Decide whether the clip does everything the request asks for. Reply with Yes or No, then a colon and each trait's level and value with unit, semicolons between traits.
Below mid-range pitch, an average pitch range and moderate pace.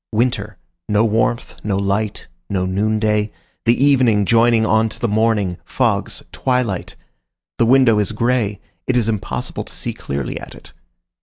No: low, 110 Hz; narrow, 2.3 semitones; average, 150 wpm